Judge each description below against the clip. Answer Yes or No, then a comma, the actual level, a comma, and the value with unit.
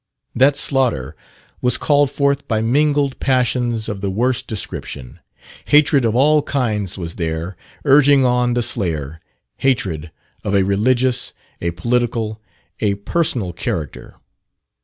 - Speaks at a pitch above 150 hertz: No, low, 120 Hz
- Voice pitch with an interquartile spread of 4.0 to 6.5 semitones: Yes, wide, 5.4 semitones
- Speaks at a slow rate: Yes, slow, 125 wpm